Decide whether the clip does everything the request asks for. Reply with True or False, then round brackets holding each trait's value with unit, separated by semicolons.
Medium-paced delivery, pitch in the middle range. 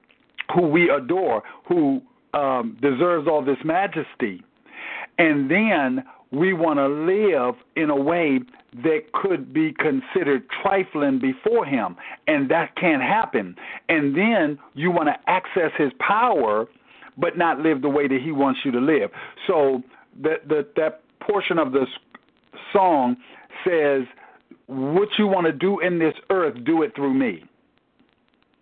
True (145 wpm; 160 Hz)